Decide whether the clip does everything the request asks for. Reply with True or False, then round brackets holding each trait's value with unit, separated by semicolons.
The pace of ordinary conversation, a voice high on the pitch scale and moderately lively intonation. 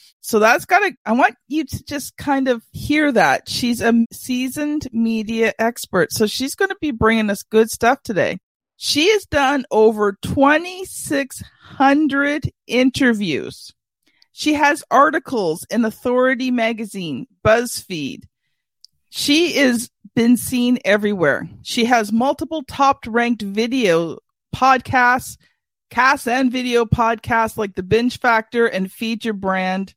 False (130 wpm; 245 Hz; 3.7 semitones)